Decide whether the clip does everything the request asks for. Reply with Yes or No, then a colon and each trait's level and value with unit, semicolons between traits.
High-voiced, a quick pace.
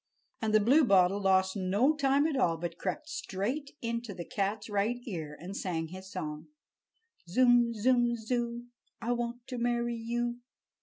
No: high, 230 Hz; average, 155 wpm